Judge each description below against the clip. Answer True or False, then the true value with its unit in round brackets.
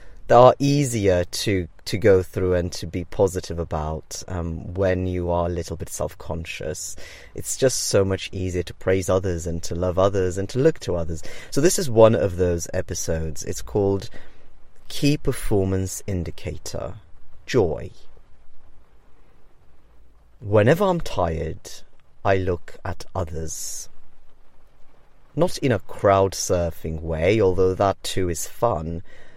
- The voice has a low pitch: True (90 Hz)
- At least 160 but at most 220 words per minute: False (140 wpm)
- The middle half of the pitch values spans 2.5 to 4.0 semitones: True (2.9 semitones)